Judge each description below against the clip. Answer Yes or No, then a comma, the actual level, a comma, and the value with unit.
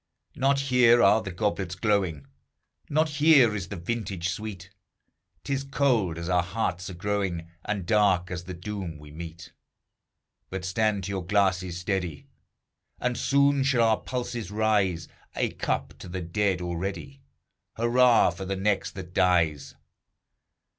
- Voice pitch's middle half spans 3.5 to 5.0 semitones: Yes, average, 4.4 semitones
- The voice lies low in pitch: Yes, very low, 95 Hz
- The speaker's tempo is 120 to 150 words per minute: Yes, average, 145 wpm